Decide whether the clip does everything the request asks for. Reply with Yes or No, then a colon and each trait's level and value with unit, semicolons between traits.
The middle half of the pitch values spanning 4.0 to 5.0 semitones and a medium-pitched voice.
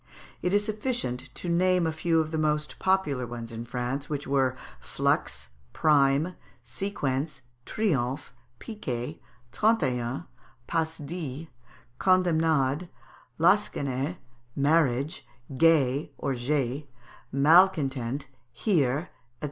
Yes: average, 4.6 semitones; medium, 150 Hz